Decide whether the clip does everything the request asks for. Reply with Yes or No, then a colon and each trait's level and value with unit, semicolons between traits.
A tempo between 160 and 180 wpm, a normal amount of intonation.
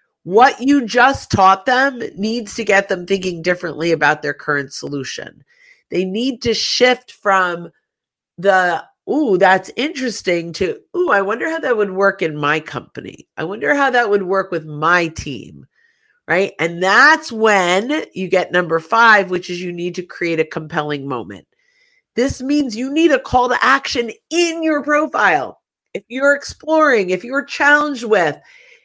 No: average, 165 wpm; wide, 7.9 semitones